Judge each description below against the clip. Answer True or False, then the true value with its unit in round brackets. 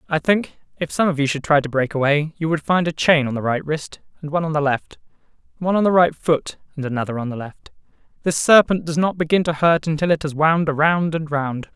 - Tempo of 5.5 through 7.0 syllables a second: True (5.9 syllables/s)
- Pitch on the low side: False (155 Hz)